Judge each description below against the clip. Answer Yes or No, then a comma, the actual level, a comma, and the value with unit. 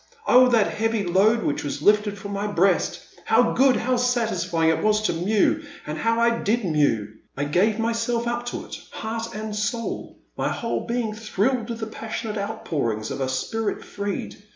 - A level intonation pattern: No, average, 3.9 semitones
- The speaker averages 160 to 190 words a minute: Yes, average, 185 wpm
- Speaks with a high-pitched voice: Yes, high, 215 Hz